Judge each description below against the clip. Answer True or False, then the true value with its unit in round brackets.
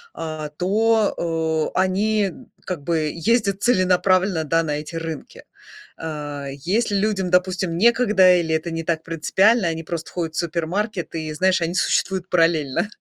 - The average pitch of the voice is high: False (175 Hz)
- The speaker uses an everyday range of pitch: True (3.1 semitones)